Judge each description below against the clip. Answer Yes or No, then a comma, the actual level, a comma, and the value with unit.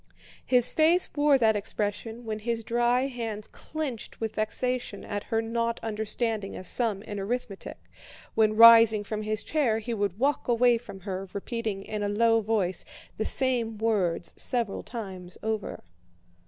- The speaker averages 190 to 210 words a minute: No, average, 155 wpm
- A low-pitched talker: No, high, 225 Hz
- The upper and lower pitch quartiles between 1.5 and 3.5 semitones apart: Yes, narrow, 2.5 semitones